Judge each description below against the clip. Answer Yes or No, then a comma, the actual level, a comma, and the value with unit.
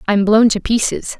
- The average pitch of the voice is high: Yes, high, 215 Hz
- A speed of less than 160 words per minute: No, average, 200 wpm